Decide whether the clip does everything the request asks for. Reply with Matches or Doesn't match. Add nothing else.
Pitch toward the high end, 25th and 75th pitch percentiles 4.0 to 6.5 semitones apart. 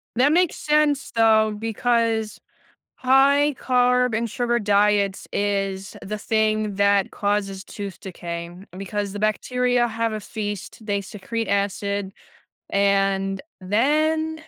Doesn't match